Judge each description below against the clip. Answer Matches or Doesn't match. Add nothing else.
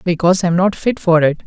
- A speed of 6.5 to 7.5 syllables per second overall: Matches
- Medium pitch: Matches